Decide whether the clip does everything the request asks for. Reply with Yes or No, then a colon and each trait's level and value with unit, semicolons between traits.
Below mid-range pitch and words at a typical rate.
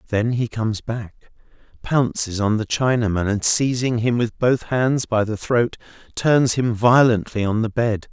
Yes: low, 115 Hz; average, 170 wpm